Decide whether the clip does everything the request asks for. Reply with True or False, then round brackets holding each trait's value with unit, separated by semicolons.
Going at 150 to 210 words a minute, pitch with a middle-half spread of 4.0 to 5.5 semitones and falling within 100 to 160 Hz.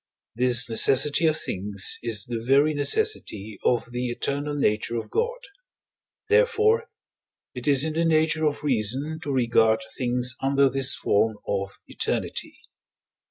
False (135 wpm; 5.0 semitones; 135 Hz)